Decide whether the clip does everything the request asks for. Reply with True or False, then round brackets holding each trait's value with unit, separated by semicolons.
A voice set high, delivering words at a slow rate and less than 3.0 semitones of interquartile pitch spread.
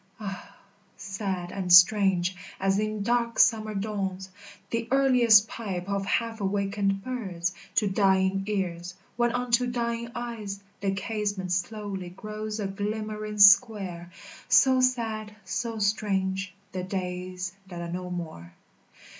True (200 Hz; 125 wpm; 2.6 semitones)